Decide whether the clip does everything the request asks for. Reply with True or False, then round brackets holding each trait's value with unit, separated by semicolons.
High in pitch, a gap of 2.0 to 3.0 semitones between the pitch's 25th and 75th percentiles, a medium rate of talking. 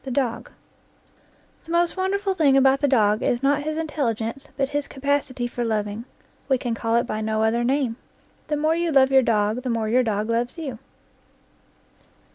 False (260 Hz; 4.1 semitones; 185 wpm)